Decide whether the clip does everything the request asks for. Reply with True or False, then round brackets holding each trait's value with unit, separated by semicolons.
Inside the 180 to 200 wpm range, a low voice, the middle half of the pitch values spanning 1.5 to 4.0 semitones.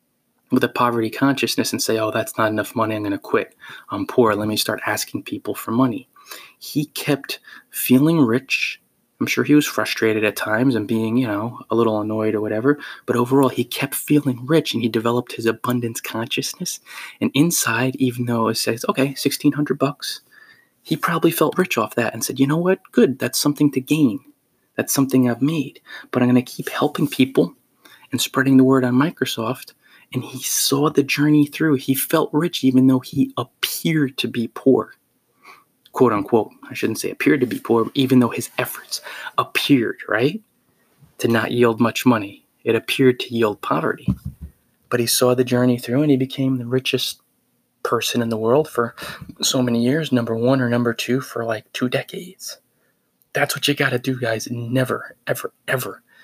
True (190 wpm; 125 Hz; 3.1 semitones)